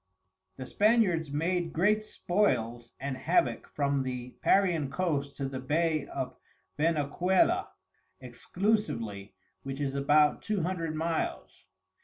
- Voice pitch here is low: No, medium, 150 Hz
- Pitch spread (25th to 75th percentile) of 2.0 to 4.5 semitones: No, average, 4.9 semitones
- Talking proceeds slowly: Yes, slow, 115 wpm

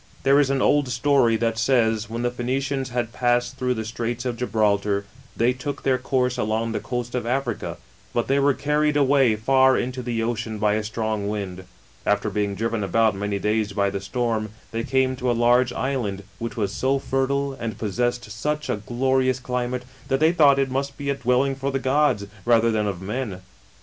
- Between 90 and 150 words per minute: No, average, 200 wpm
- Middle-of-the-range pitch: No, low, 120 Hz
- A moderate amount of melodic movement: Yes, average, 3.3 semitones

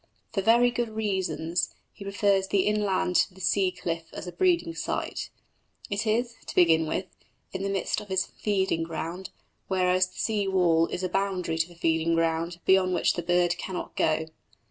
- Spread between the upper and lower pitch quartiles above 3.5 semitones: No, average, 2.9 semitones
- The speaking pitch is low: No, medium, 185 Hz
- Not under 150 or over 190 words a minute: Yes, average, 185 wpm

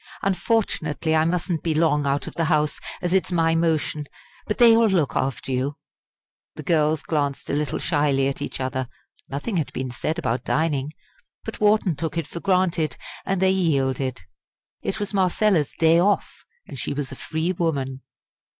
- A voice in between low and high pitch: Yes, medium, 160 Hz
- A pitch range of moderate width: Yes, average, 4.0 semitones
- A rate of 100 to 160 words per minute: No, average, 175 wpm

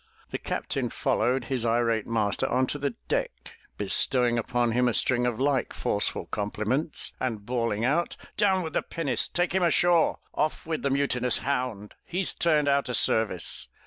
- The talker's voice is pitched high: No, low, 125 Hz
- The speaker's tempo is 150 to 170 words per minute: Yes, average, 165 wpm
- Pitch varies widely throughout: No, average, 4.1 semitones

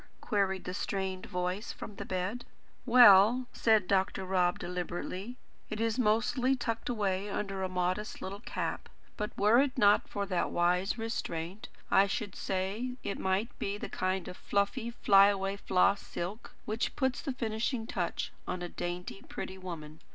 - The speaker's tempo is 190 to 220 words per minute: No, average, 160 wpm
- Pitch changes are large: No, average, 3.2 semitones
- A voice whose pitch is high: Yes, high, 200 Hz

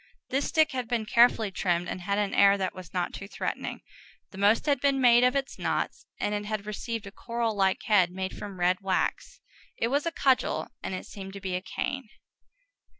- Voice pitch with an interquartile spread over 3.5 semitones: Yes, average, 4.4 semitones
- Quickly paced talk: Yes, fast, 210 wpm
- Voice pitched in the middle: No, high, 210 Hz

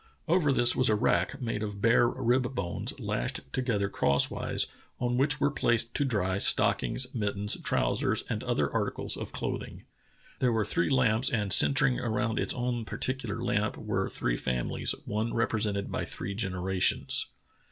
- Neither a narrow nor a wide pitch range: Yes, average, 3.8 semitones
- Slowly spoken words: No, average, 155 wpm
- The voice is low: Yes, low, 115 Hz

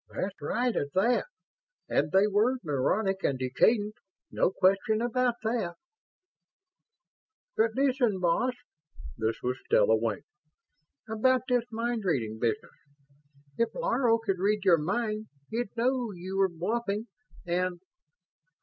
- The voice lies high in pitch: Yes, high, 205 Hz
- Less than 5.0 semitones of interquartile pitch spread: No, average, 5.3 semitones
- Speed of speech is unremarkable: No, slow, 120 wpm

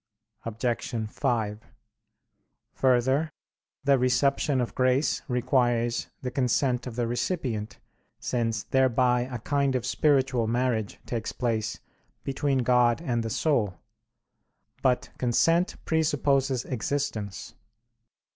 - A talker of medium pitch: No, low, 125 Hz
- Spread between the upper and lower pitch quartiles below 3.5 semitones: Yes, narrow, 2.5 semitones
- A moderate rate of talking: No, slow, 100 wpm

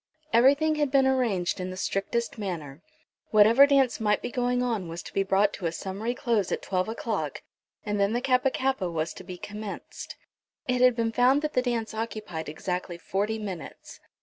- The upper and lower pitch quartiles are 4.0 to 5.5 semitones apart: Yes, average, 5.0 semitones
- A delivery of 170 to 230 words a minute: Yes, average, 190 wpm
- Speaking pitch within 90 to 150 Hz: No, high, 220 Hz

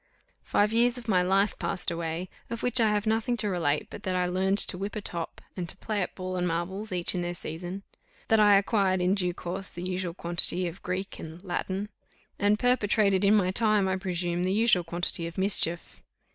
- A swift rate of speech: Yes, fast, 215 wpm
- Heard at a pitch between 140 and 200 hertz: Yes, high, 190 Hz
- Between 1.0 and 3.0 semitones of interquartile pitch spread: Yes, average, 2.7 semitones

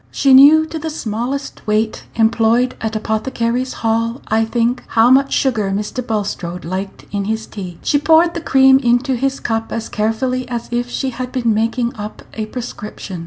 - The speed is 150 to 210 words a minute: Yes, average, 175 wpm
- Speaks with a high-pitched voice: Yes, high, 235 Hz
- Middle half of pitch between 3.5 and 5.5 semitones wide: No, average, 3.1 semitones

